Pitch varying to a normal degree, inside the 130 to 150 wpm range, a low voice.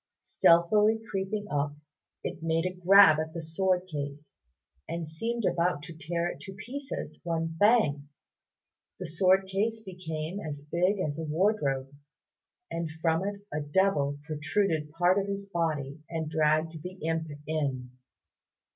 No: average, 3.8 semitones; average, 145 wpm; medium, 165 Hz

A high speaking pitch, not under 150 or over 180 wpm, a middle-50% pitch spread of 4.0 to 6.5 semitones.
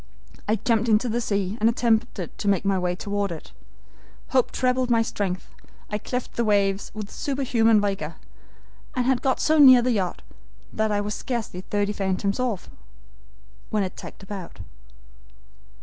No: high, 210 Hz; average, 160 wpm; average, 3.4 semitones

